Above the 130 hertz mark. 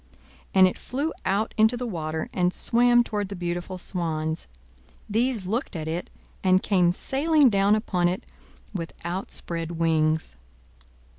Yes: medium, 185 Hz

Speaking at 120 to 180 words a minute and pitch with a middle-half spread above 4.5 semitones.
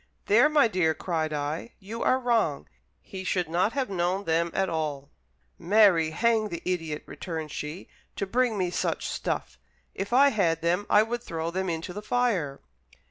Yes: average, 175 wpm; average, 5.2 semitones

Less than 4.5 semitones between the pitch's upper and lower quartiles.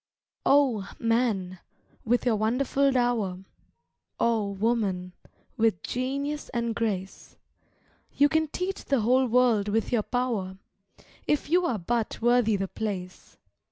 Yes: average, 3.9 semitones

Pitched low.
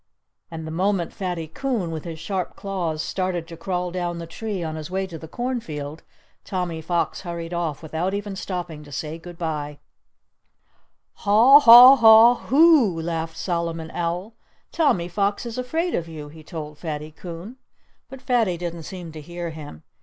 No: medium, 175 Hz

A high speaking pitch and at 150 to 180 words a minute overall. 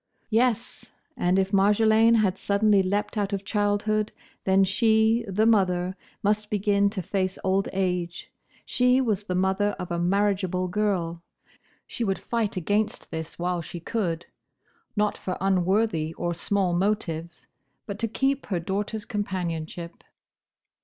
No: high, 195 Hz; average, 140 wpm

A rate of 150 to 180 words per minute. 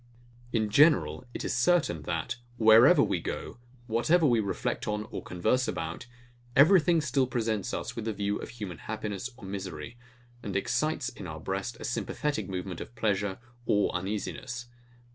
Yes: average, 160 wpm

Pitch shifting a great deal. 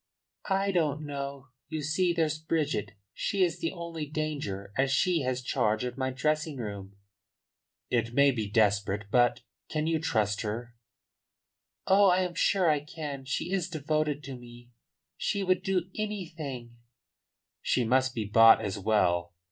Yes: wide, 5.8 semitones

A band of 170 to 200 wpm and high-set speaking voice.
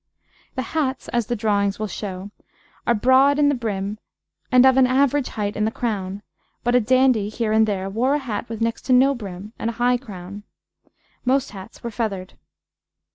Yes: average, 190 wpm; high, 230 Hz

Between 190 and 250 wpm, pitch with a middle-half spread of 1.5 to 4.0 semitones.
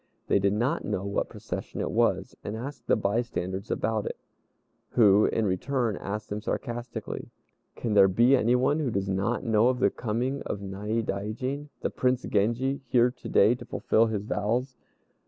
No: average, 170 wpm; average, 3.6 semitones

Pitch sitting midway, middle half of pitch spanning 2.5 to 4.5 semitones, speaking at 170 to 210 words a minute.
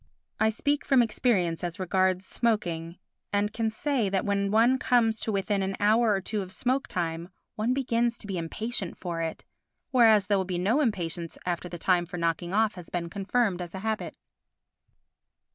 No: high, 200 Hz; average, 4.1 semitones; average, 185 wpm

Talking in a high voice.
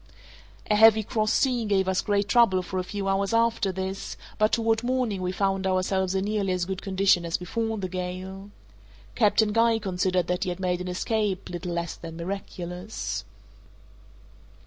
Yes: high, 195 Hz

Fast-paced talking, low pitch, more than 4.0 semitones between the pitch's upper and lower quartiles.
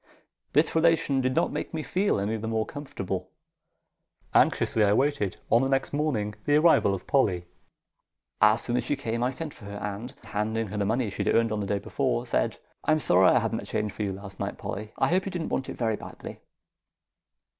Yes: fast, 215 wpm; low, 115 Hz; wide, 5.6 semitones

